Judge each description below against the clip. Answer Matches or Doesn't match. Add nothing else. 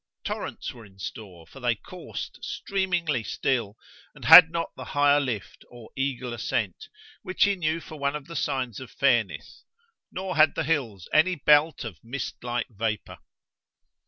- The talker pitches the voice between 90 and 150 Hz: Matches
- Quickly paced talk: Doesn't match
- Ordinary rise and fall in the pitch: Doesn't match